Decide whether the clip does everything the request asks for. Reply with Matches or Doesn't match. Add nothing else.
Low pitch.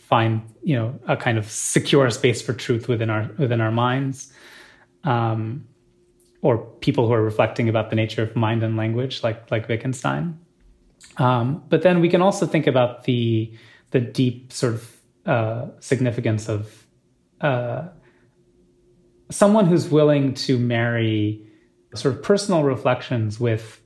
Matches